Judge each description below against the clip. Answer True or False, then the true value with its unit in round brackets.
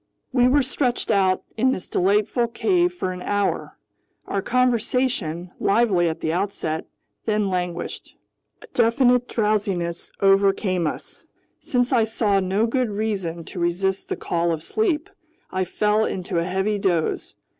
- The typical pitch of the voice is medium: False (200 Hz)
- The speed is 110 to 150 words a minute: True (145 wpm)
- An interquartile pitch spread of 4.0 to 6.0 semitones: True (4.7 semitones)